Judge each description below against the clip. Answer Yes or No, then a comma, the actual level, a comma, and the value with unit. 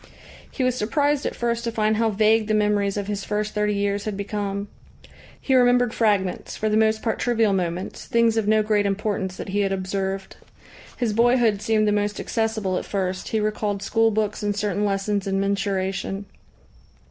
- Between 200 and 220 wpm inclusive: No, average, 185 wpm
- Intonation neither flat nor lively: No, narrow, 1.9 semitones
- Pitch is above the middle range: Yes, high, 210 Hz